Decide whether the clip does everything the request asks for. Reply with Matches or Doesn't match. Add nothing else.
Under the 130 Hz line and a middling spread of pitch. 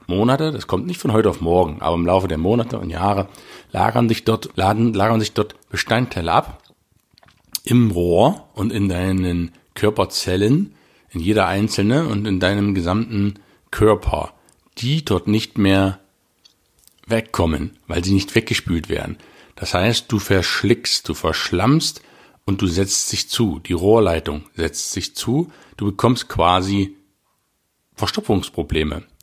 Matches